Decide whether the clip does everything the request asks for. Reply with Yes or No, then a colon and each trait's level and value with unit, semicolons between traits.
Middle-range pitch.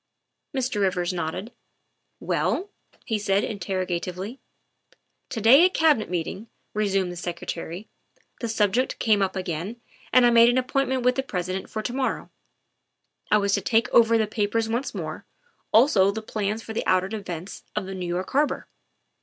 No: high, 210 Hz